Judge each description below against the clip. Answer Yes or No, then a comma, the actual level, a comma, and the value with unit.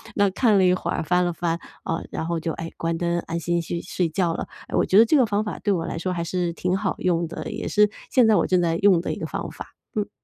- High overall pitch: No, medium, 180 Hz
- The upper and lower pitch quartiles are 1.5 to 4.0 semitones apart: Yes, average, 3.2 semitones